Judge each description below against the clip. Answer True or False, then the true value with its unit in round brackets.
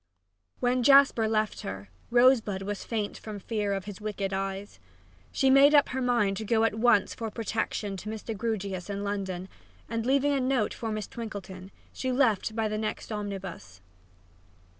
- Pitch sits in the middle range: False (215 Hz)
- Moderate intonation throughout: True (3.2 semitones)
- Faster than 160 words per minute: True (170 wpm)